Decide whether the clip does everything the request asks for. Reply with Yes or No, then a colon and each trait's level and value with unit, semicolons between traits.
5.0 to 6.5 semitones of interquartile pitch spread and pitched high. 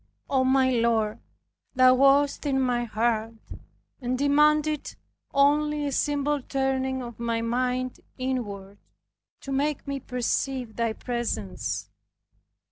No: average, 3.0 semitones; very high, 255 Hz